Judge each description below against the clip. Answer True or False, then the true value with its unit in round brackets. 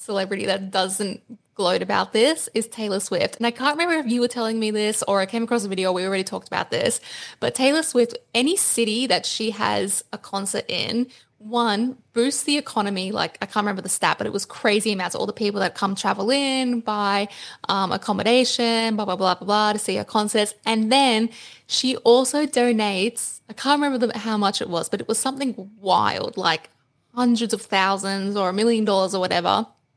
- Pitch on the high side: True (220 Hz)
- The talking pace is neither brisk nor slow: False (210 wpm)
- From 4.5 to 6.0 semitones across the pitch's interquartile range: False (3.4 semitones)